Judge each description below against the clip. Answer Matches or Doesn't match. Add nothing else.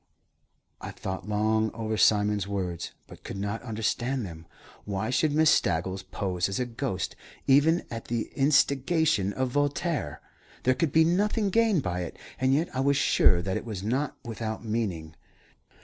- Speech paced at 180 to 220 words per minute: Doesn't match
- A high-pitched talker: Doesn't match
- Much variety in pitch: Matches